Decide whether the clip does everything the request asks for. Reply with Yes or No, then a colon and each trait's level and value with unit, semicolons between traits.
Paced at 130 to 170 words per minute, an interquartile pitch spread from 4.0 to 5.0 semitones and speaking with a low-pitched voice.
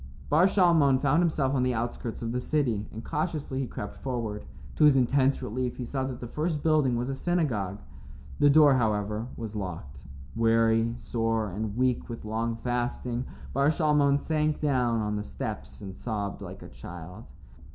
No: average, 180 wpm; average, 4.3 semitones; low, 125 Hz